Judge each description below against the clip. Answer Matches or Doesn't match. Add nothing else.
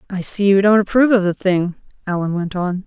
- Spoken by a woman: Matches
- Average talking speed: Doesn't match